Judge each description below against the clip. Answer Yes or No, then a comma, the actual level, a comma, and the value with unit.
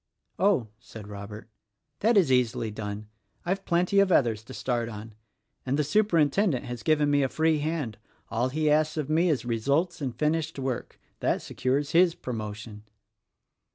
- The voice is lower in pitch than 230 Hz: Yes, medium, 140 Hz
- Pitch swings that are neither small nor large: No, wide, 5.8 semitones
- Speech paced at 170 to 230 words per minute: No, average, 160 wpm